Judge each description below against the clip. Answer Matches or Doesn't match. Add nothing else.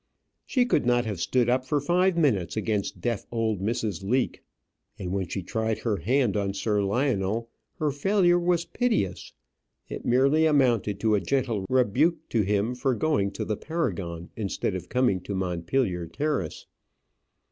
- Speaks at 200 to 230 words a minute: Doesn't match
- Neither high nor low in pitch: Doesn't match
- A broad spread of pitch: Matches